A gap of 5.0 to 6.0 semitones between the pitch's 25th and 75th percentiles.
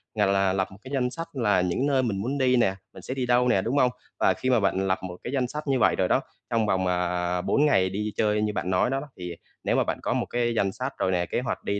Yes: average, 5.3 semitones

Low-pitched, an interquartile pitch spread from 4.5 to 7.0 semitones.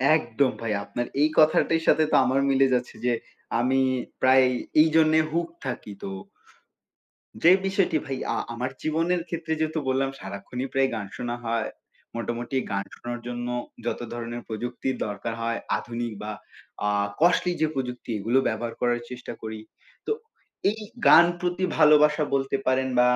Yes: low, 130 Hz; average, 4.8 semitones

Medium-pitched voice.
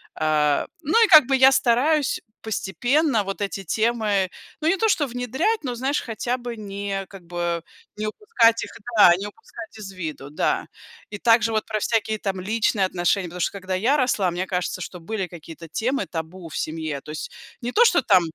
No: high, 210 Hz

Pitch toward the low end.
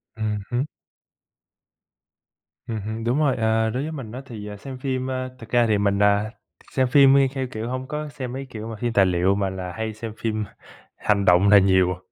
Yes: low, 110 Hz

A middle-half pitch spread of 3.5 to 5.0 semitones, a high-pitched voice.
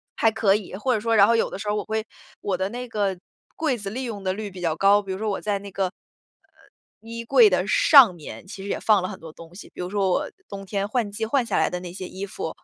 No: average, 2.9 semitones; high, 205 Hz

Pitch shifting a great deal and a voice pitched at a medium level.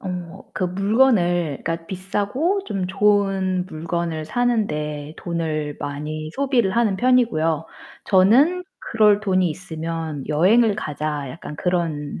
No: average, 5.0 semitones; medium, 180 Hz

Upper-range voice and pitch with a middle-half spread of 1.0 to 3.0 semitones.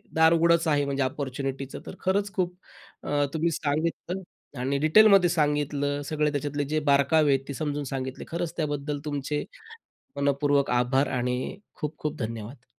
No: medium, 145 Hz; narrow, 2.6 semitones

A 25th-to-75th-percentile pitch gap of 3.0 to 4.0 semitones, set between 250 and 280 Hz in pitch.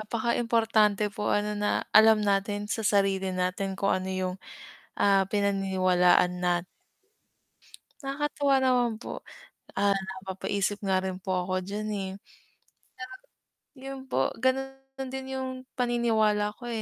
No: average, 3.7 semitones; high, 205 Hz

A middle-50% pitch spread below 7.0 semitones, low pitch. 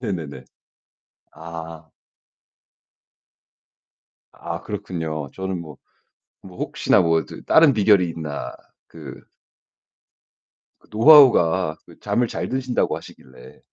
Yes: average, 5.2 semitones; very low, 85 Hz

